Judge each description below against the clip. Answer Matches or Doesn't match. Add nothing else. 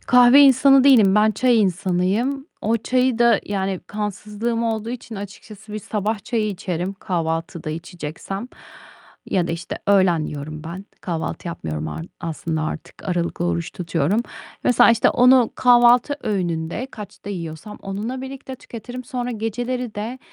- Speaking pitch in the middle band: Doesn't match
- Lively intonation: Matches